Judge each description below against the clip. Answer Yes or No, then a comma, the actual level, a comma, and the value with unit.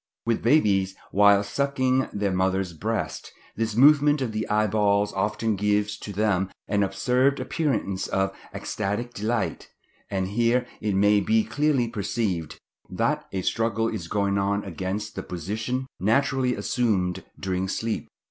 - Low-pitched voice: Yes, low, 105 Hz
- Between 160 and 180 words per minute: No, average, 140 wpm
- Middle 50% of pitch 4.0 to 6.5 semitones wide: No, average, 3.4 semitones